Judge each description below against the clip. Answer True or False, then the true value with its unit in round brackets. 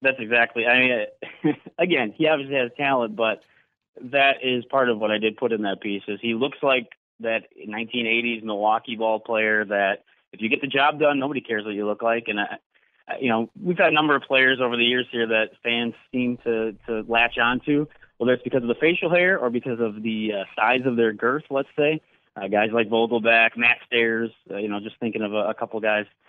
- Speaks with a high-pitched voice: False (115 Hz)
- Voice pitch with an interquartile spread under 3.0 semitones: False (3.3 semitones)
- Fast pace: True (225 wpm)